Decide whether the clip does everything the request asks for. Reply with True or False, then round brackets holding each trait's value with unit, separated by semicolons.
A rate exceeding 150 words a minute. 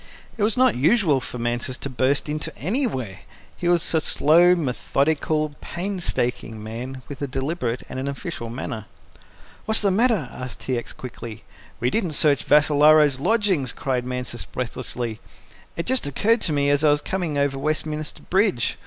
True (160 wpm)